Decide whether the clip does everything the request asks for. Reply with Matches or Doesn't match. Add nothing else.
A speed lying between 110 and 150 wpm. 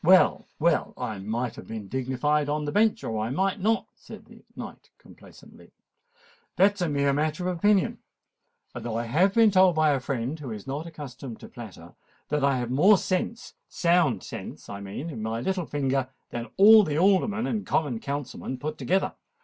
Doesn't match